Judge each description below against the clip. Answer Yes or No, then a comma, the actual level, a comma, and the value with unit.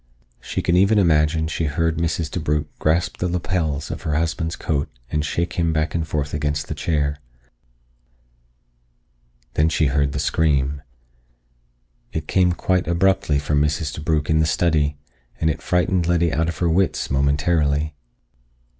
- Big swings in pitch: No, narrow, 2.5 semitones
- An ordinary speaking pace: Yes, average, 155 wpm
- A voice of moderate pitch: No, very low, 80 Hz